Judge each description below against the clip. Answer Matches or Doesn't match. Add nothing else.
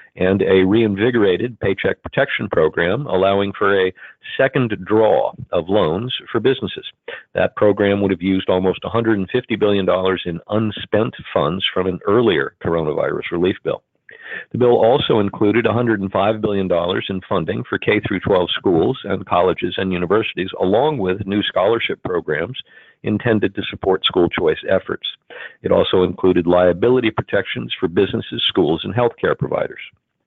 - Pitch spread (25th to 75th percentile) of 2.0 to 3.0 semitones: Matches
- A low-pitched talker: Matches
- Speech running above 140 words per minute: Doesn't match